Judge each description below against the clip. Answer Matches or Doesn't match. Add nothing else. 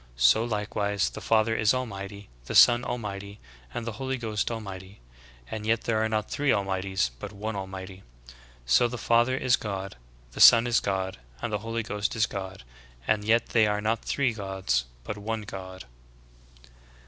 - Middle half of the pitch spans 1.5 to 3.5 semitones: Matches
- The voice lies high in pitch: Doesn't match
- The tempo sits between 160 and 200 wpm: Matches